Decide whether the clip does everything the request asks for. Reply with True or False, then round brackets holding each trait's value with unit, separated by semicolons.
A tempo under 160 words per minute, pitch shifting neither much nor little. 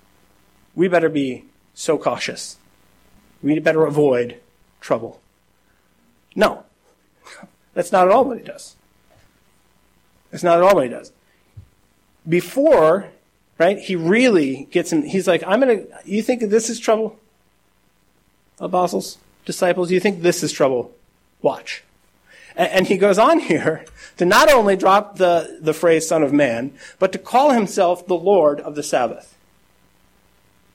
True (140 wpm; 4.4 semitones)